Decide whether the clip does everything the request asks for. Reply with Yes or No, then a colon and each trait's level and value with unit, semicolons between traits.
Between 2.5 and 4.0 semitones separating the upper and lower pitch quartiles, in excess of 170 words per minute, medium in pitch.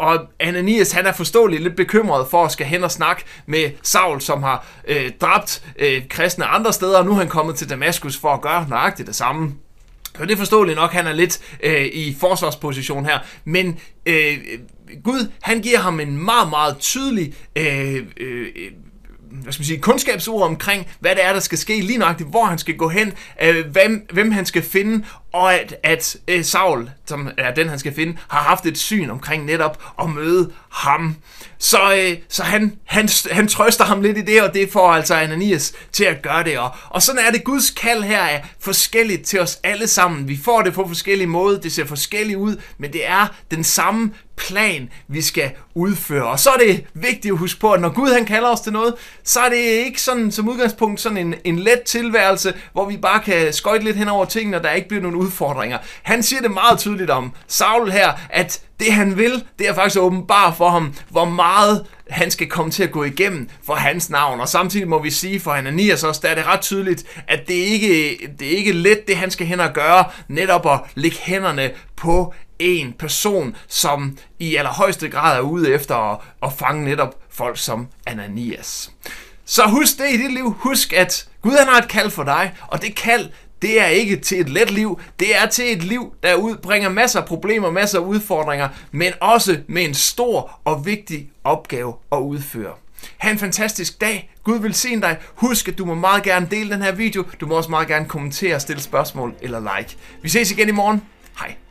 No: average, 5.1 semitones; average, 210 wpm; medium, 180 Hz